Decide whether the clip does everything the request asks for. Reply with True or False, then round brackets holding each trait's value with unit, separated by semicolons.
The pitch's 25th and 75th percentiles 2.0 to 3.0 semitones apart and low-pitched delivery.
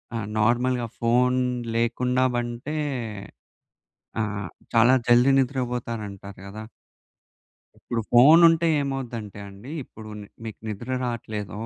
True (2.6 semitones; 120 Hz)